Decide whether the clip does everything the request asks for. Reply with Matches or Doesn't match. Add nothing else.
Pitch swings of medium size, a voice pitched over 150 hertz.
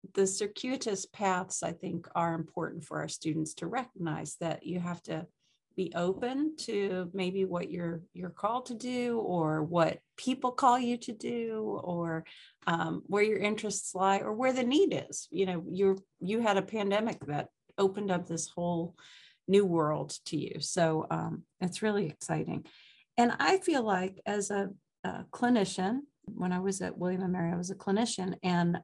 Matches